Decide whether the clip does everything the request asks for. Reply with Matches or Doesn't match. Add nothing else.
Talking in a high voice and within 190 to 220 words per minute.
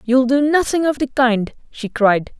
Matches